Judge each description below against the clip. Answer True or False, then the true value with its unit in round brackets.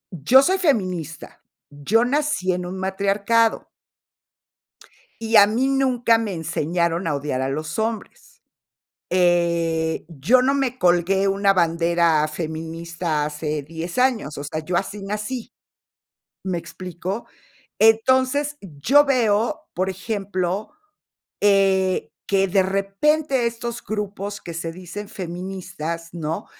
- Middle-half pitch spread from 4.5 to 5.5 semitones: True (5.1 semitones)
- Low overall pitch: False (190 Hz)